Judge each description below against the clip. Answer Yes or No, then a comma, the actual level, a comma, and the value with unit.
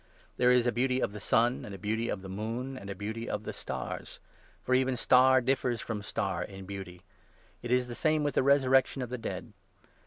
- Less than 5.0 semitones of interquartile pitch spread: Yes, average, 3.8 semitones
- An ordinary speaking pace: No, fast, 220 wpm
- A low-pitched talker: Yes, low, 120 Hz